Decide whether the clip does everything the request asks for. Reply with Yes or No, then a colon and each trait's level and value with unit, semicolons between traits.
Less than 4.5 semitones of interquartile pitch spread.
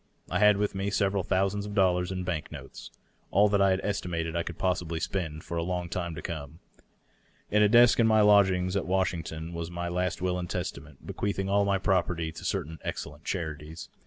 Yes: average, 2.9 semitones